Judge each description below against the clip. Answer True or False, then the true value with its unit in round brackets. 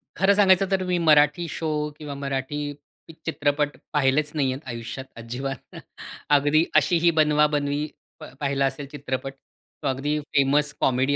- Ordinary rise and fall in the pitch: False (2.0 semitones)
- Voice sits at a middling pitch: True (145 Hz)